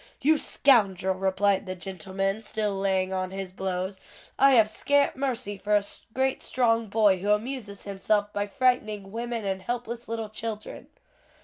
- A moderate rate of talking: Yes, average, 150 wpm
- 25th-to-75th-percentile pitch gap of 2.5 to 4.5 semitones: Yes, average, 3.1 semitones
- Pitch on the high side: Yes, high, 205 Hz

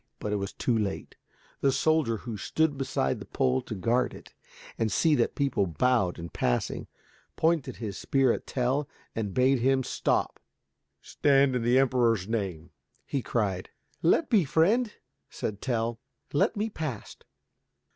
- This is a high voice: No, low, 125 Hz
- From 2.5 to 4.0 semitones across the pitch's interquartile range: No, average, 5.1 semitones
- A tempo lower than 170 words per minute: Yes, average, 155 wpm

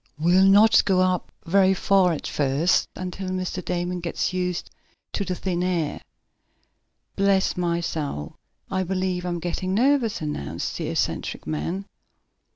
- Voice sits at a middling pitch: Yes, medium, 180 Hz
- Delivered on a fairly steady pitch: Yes, narrow, 2.0 semitones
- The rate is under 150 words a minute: Yes, average, 140 wpm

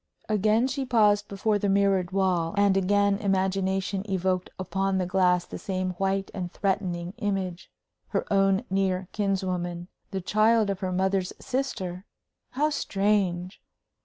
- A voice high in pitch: Yes, high, 195 Hz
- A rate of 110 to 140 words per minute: Yes, slow, 135 wpm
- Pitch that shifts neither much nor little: No, narrow, 1.7 semitones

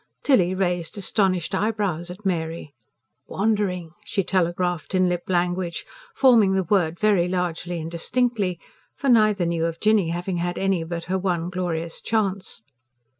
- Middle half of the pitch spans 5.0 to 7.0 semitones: No, narrow, 2.6 semitones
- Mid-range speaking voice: Yes, medium, 180 Hz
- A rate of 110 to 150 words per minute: Yes, average, 145 wpm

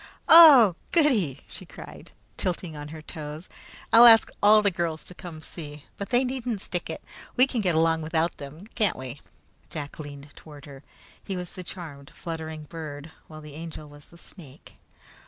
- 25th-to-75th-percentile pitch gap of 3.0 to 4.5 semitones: No, average, 4.9 semitones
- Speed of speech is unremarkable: Yes, average, 175 wpm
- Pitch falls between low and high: Yes, medium, 165 Hz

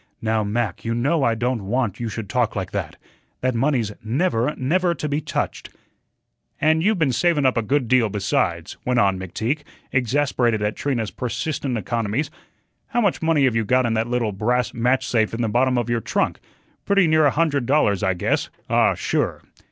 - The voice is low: Yes, low, 120 Hz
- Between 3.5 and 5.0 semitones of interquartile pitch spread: Yes, average, 4.6 semitones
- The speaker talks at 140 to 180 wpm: No, average, 190 wpm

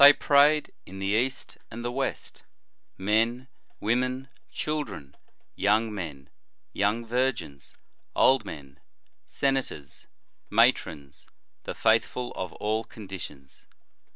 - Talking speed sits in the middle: No, slow, 110 wpm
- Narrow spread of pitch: No, wide, 5.4 semitones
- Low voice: Yes, low, 110 Hz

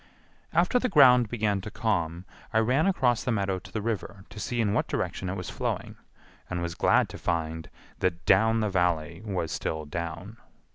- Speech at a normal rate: Yes, average, 190 wpm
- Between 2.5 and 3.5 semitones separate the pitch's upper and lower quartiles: No, average, 4.6 semitones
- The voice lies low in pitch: Yes, low, 100 Hz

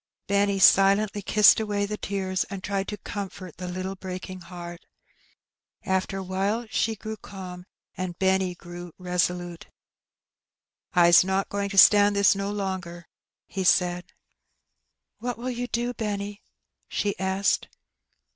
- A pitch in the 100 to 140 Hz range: No, high, 195 Hz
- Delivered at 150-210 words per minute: No, slow, 135 wpm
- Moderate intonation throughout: No, narrow, 2.0 semitones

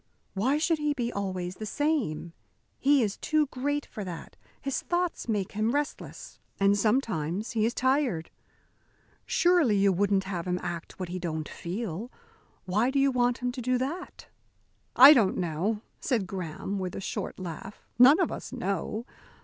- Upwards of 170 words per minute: No, average, 165 wpm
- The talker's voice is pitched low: No, high, 220 Hz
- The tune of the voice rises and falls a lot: Yes, wide, 6.2 semitones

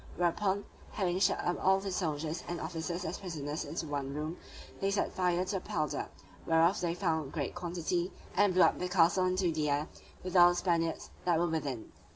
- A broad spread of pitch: No, narrow, 2.4 semitones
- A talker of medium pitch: Yes, medium, 175 Hz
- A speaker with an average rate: Yes, average, 195 wpm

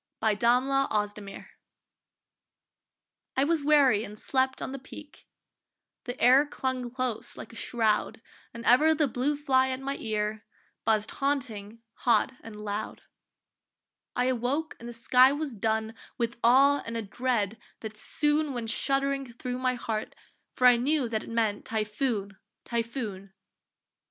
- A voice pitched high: Yes, high, 245 Hz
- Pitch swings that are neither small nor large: Yes, average, 3.6 semitones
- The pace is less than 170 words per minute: Yes, average, 145 wpm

